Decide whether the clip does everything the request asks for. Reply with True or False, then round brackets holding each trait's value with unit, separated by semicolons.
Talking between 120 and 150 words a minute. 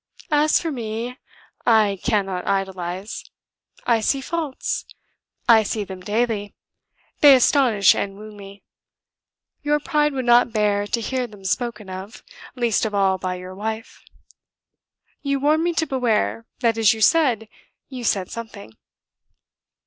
True (140 wpm)